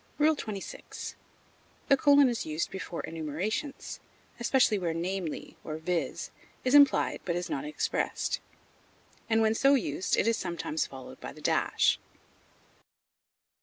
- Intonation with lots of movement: Yes, wide, 8.0 semitones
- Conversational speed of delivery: No, slow, 130 wpm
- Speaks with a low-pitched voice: No, high, 210 Hz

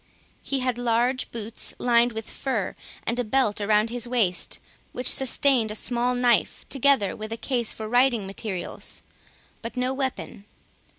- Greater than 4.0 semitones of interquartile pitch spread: No, narrow, 2.5 semitones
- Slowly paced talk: No, average, 155 wpm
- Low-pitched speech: No, high, 240 Hz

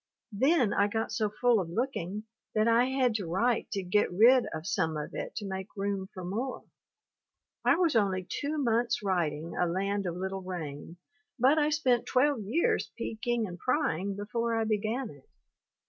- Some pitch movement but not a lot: Yes, average, 4.6 semitones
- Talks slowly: No, average, 180 wpm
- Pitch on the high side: Yes, high, 210 Hz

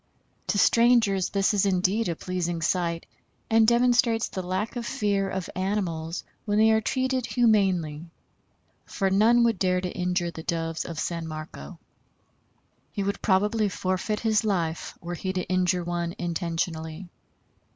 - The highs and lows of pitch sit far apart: No, average, 3.8 semitones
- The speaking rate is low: No, average, 150 wpm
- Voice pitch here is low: No, medium, 185 Hz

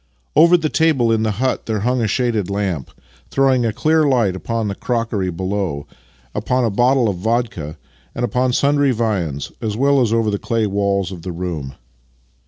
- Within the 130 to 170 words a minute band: No, average, 185 wpm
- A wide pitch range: No, average, 4.4 semitones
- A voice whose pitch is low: Yes, low, 110 Hz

